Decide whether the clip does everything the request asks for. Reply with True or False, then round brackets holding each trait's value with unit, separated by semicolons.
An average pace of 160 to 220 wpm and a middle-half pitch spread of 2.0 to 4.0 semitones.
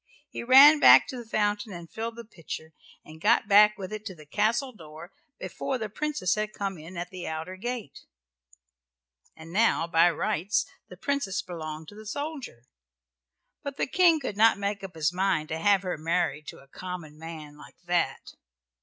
False (185 wpm; 5.2 semitones)